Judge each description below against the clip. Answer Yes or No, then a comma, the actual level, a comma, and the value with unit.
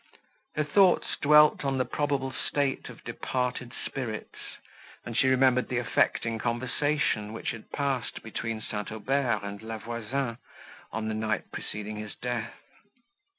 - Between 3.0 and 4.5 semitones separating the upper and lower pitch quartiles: Yes, average, 3.6 semitones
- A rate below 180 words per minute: Yes, average, 140 wpm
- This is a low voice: Yes, low, 120 Hz